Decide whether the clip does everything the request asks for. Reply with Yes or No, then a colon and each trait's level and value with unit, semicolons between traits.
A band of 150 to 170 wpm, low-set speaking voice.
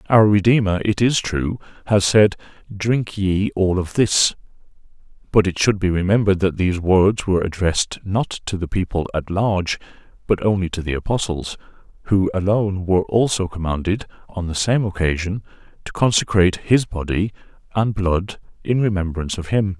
Yes: average, 160 wpm; very low, 95 Hz